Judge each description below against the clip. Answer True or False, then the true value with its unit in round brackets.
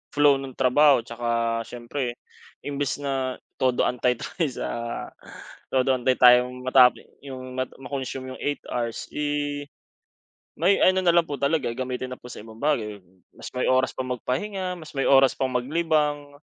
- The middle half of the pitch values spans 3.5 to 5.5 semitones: False (2.6 semitones)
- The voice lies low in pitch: True (130 Hz)